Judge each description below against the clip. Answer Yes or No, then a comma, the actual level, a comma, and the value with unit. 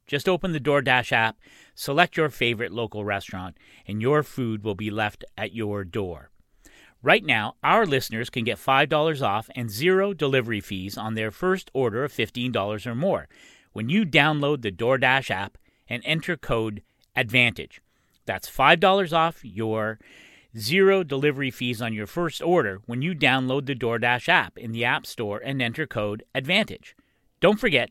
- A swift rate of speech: No, average, 165 wpm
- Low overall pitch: Yes, low, 125 Hz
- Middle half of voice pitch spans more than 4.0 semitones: Yes, wide, 5.5 semitones